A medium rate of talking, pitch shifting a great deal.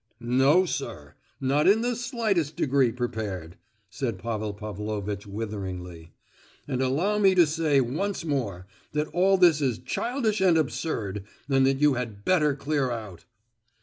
Yes: average, 145 wpm; wide, 7.5 semitones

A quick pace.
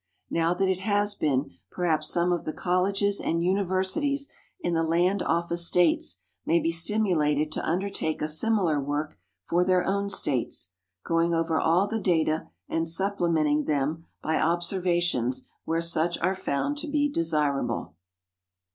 No: average, 150 wpm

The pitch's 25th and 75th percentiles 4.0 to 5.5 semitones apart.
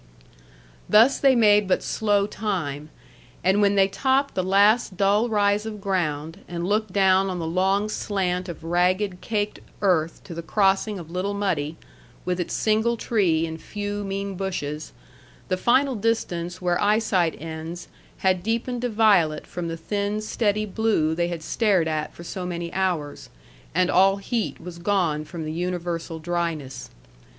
No: average, 3.5 semitones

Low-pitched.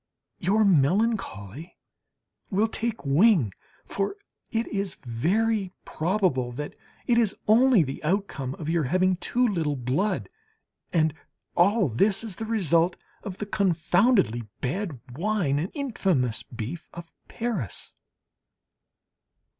No: medium, 185 Hz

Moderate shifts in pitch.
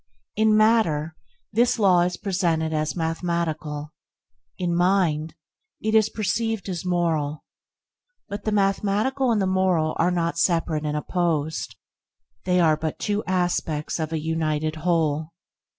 Yes: average, 3.8 semitones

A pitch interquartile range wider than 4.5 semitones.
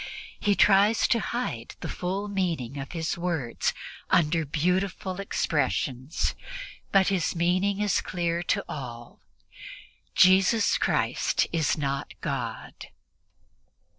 Yes: average, 5.0 semitones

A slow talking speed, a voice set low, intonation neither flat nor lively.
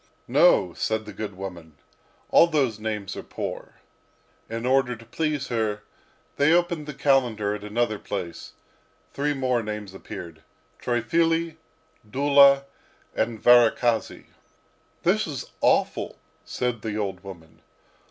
Yes: slow, 125 wpm; low, 115 Hz; average, 4.9 semitones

